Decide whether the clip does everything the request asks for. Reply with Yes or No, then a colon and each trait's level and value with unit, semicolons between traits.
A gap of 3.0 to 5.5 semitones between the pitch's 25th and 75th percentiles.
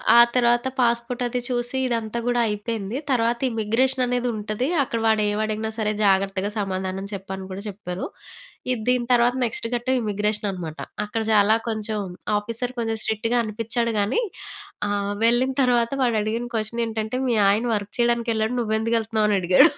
No: narrow, 2.5 semitones